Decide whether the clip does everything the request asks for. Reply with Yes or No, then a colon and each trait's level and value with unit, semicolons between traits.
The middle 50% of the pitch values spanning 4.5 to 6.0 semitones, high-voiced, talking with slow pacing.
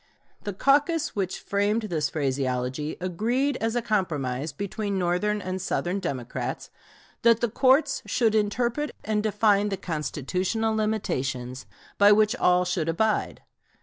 Yes: average, 5.0 semitones; high, 200 Hz; slow, 130 wpm